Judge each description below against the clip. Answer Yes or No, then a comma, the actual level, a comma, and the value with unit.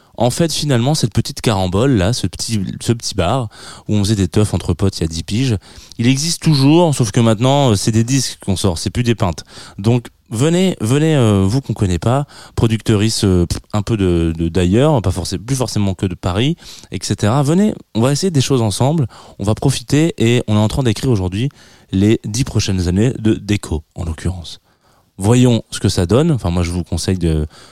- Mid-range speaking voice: No, low, 110 Hz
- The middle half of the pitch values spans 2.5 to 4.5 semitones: No, wide, 5.4 semitones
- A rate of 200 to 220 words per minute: Yes, average, 210 wpm